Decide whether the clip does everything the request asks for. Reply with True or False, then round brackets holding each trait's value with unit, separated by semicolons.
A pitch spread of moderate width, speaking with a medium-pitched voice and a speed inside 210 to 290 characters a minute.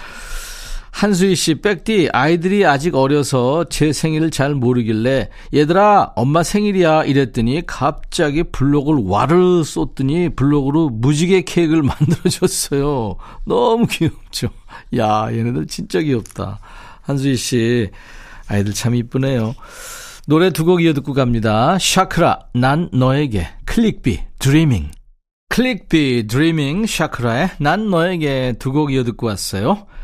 False (5.8 semitones; 145 Hz; 275 characters per minute)